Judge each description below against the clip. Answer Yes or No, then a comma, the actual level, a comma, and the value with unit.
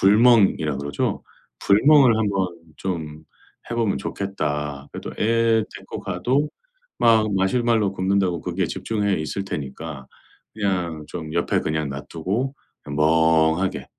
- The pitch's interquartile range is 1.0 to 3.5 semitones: No, wide, 5.6 semitones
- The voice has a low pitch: Yes, very low, 95 Hz